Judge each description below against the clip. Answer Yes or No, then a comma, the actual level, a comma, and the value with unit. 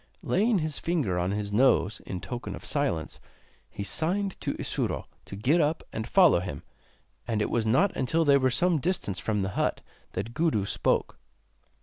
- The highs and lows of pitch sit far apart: Yes, wide, 8.3 semitones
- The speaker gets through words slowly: No, average, 180 wpm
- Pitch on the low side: Yes, low, 125 Hz